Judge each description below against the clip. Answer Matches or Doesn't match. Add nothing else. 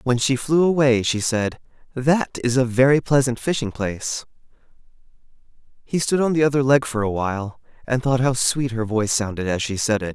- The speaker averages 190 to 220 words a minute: Matches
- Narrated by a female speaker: Doesn't match